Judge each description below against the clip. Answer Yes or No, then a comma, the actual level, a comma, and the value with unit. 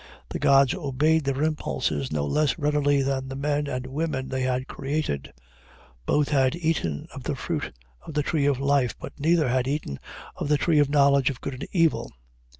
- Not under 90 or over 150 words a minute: No, average, 190 wpm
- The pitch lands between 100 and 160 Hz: Yes, medium, 140 Hz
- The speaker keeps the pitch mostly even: Yes, narrow, 2.3 semitones